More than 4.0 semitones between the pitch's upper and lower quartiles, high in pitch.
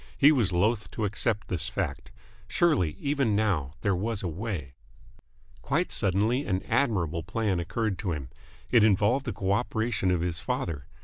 No: average, 4.7 semitones; low, 100 Hz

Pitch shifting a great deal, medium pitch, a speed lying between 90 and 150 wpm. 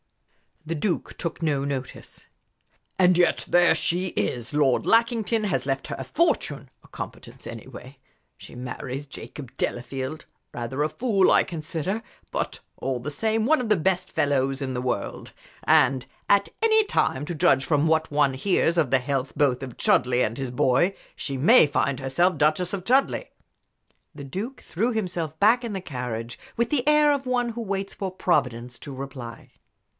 No: wide, 7.0 semitones; medium, 155 Hz; average, 170 wpm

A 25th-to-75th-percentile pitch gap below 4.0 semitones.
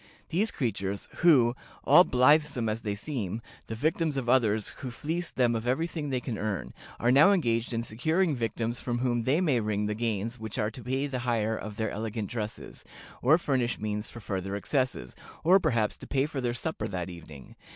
No: average, 4.3 semitones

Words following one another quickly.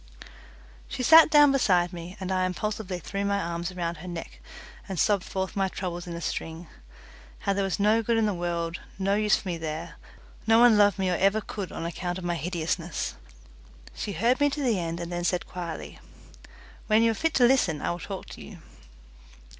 Yes: fast, 210 wpm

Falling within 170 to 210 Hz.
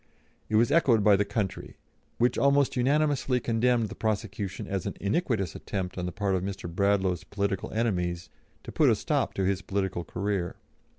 No: low, 100 Hz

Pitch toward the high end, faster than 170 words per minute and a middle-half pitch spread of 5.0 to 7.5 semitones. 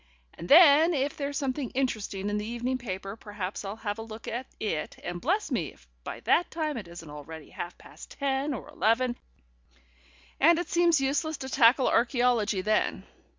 Yes: high, 240 Hz; average, 180 wpm; wide, 5.4 semitones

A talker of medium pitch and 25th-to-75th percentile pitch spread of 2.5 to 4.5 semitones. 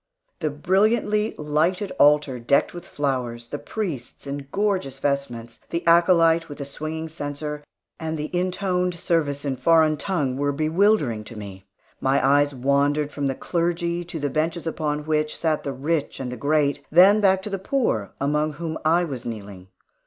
Yes: medium, 150 Hz; average, 3.6 semitones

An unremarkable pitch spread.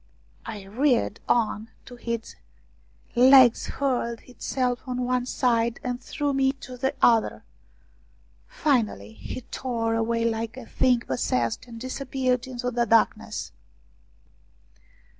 No: narrow, 2.1 semitones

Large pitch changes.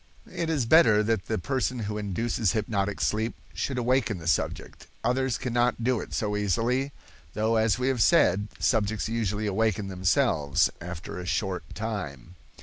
No: average, 3.6 semitones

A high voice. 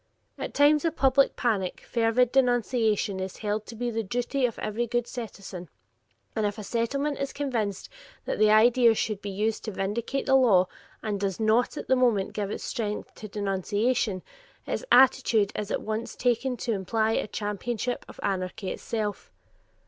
Yes: high, 225 Hz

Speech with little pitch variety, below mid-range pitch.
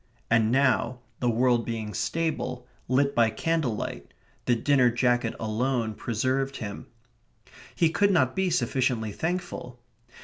No: average, 3.3 semitones; low, 125 Hz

